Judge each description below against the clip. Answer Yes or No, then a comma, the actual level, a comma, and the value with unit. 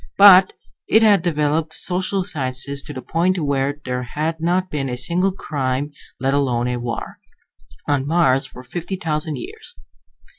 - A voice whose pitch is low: No, medium, 150 Hz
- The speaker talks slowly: No, average, 155 wpm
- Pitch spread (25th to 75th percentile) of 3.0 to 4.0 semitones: No, average, 4.9 semitones